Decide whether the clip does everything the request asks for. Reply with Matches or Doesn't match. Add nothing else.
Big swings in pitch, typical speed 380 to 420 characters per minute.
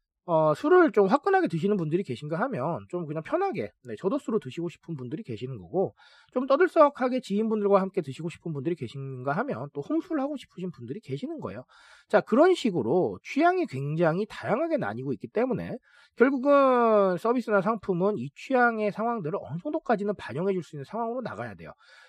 Matches